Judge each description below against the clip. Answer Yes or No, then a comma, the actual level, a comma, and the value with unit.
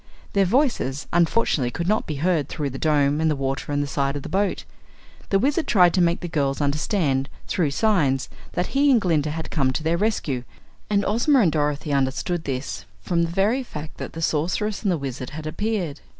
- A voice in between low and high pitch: Yes, medium, 160 Hz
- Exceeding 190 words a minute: Yes, fast, 205 wpm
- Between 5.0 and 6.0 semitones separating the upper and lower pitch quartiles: Yes, wide, 5.6 semitones